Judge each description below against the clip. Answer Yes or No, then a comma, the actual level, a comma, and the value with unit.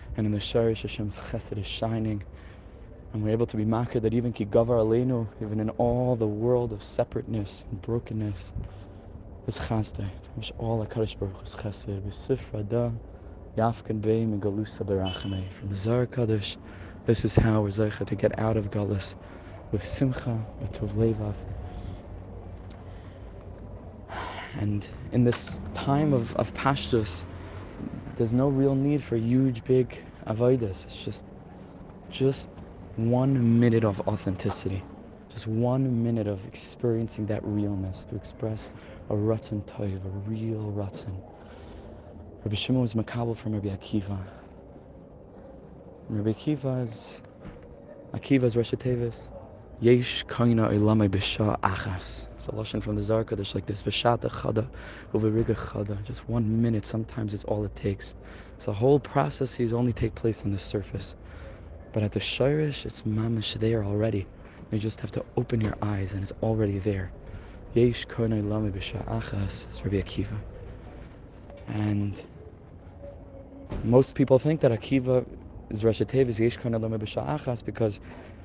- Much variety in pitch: No, average, 2.9 semitones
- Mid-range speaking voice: No, low, 105 Hz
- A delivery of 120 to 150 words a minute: Yes, average, 140 wpm